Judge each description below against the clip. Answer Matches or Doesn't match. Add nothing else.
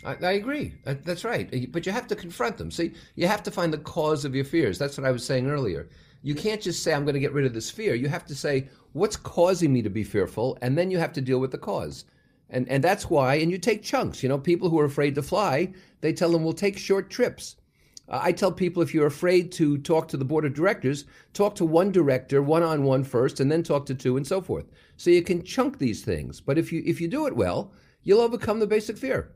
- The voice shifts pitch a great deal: Doesn't match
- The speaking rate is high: Matches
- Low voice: Doesn't match